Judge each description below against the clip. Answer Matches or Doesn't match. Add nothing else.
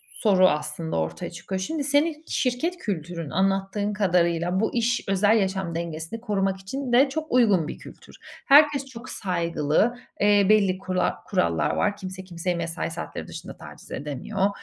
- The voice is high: Matches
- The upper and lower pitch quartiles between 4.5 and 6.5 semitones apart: Matches